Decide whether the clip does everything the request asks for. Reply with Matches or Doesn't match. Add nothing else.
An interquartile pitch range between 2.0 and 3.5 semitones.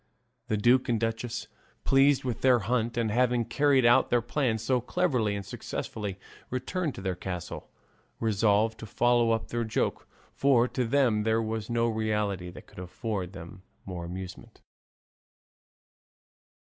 Matches